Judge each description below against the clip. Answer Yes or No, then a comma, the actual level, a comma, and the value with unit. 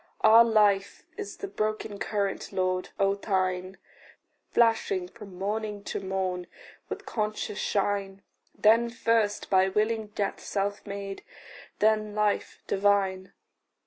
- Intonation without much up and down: Yes, narrow, 1.8 semitones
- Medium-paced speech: No, slow, 115 wpm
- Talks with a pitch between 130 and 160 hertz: No, high, 205 Hz